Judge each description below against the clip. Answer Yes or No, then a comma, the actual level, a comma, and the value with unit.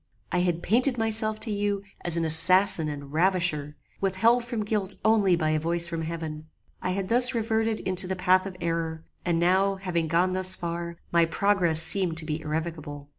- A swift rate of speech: No, average, 185 wpm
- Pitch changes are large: No, average, 3.5 semitones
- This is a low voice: No, medium, 180 Hz